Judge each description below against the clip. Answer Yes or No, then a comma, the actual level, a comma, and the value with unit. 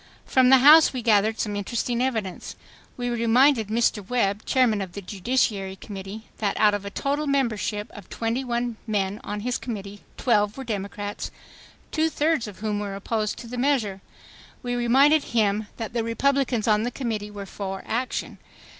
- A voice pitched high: Yes, high, 225 Hz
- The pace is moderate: Yes, average, 170 wpm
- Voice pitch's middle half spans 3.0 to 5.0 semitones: Yes, average, 3.3 semitones